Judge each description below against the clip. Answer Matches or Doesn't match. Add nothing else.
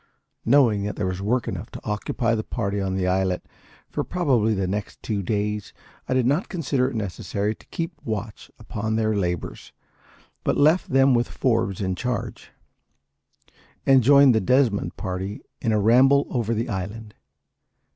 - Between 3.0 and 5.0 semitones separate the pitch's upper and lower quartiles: Matches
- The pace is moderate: Matches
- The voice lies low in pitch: Matches